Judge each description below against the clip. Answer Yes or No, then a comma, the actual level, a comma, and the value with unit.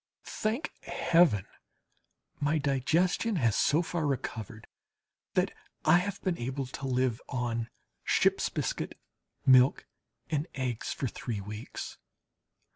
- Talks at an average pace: No, slow, 115 wpm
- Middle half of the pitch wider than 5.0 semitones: Yes, wide, 5.6 semitones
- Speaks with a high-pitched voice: No, low, 135 Hz